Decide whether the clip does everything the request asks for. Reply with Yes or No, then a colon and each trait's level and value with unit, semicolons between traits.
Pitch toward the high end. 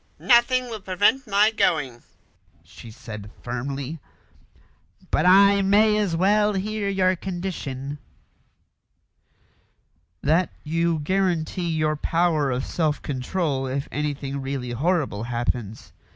No: medium, 165 Hz